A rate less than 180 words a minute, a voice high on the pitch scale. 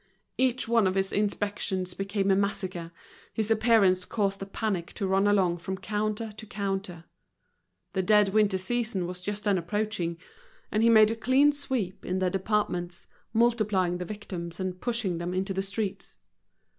Yes: average, 165 wpm; high, 200 Hz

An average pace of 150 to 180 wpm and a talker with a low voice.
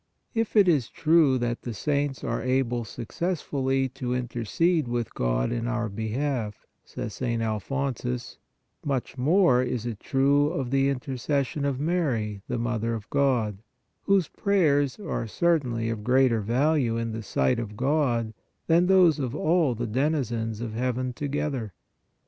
Yes: average, 160 wpm; low, 130 Hz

